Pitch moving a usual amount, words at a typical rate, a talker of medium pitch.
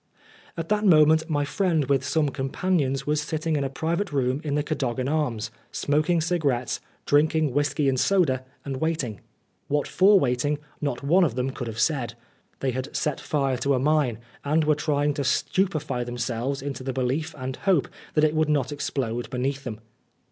Yes: average, 3.1 semitones; average, 180 wpm; medium, 145 Hz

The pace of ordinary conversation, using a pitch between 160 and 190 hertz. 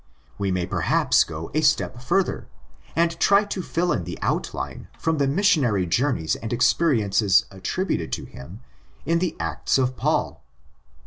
No: average, 155 wpm; low, 130 Hz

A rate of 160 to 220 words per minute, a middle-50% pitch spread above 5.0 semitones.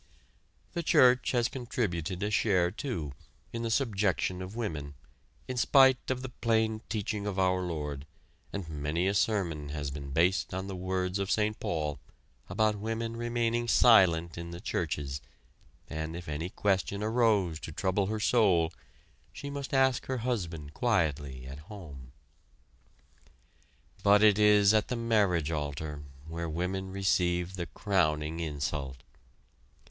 No: average, 140 wpm; wide, 5.6 semitones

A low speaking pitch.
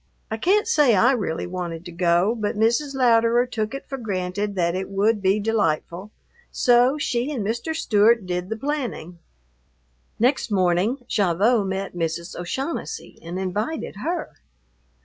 No: high, 210 Hz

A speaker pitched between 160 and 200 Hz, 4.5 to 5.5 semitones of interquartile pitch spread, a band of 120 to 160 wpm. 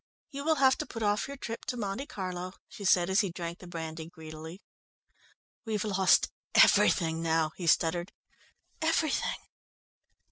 Yes: medium, 185 Hz; average, 5.2 semitones; average, 150 wpm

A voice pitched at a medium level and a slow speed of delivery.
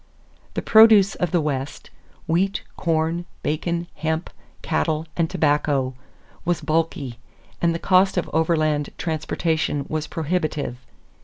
Yes: medium, 160 Hz; slow, 115 wpm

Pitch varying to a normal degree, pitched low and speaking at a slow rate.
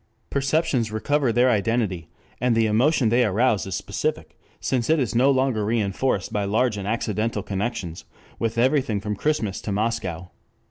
No: average, 3.8 semitones; low, 115 Hz; average, 155 wpm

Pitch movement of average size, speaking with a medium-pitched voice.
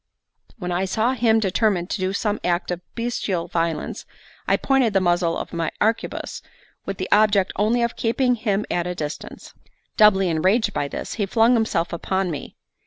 No: average, 4.1 semitones; high, 195 Hz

